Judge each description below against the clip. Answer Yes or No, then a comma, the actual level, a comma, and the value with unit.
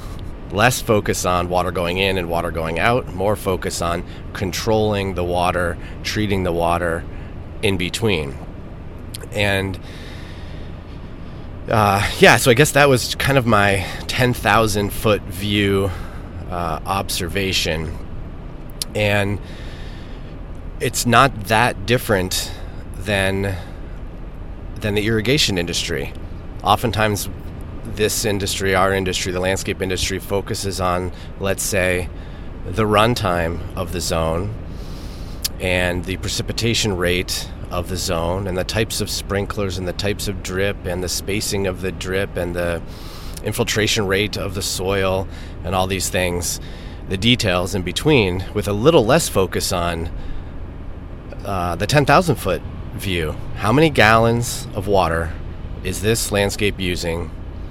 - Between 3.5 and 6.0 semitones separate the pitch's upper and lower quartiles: No, average, 3.1 semitones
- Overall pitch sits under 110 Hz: Yes, very low, 95 Hz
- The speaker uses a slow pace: Yes, slow, 130 wpm